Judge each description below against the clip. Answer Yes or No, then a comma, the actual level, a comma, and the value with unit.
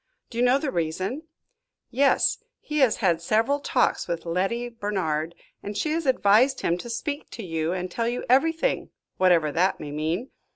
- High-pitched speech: Yes, high, 215 Hz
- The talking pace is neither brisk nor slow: Yes, average, 175 wpm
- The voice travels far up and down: Yes, wide, 7.3 semitones